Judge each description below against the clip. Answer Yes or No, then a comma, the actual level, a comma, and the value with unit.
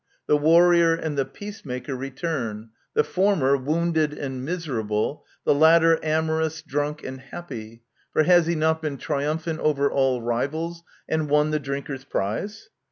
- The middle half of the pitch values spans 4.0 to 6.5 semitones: No, average, 3.5 semitones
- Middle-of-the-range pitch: Yes, medium, 150 Hz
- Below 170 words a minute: Yes, average, 155 wpm